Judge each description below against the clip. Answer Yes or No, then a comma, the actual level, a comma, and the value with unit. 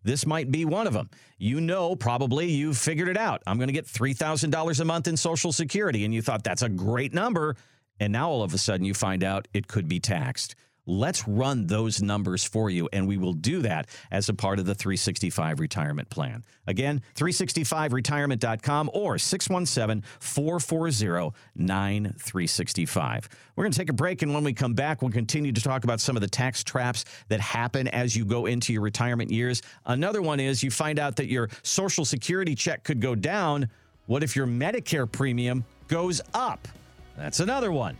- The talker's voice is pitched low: Yes, low, 130 Hz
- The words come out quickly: No, average, 195 wpm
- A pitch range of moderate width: No, wide, 6.0 semitones